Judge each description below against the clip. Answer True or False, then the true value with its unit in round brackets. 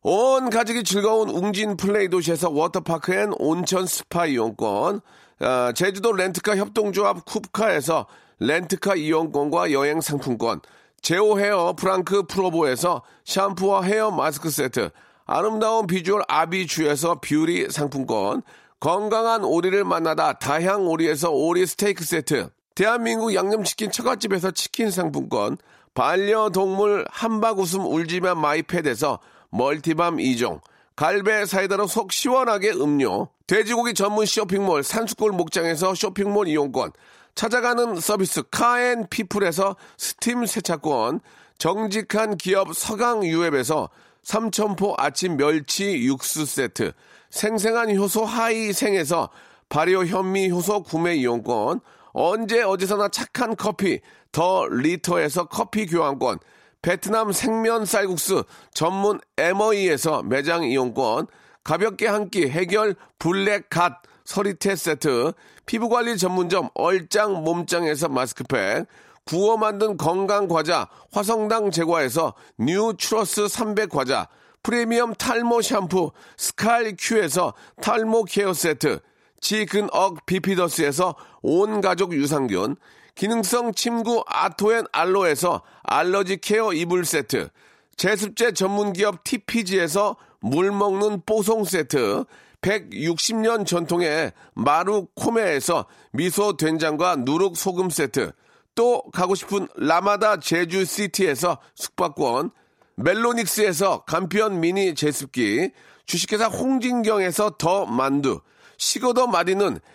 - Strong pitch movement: False (4.1 semitones)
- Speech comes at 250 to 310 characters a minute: True (265 characters per minute)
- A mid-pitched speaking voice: False (200 Hz)